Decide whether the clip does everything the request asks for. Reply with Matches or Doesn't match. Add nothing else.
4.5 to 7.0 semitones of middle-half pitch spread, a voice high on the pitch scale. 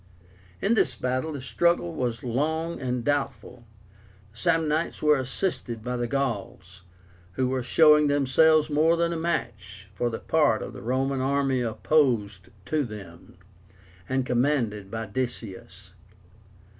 Doesn't match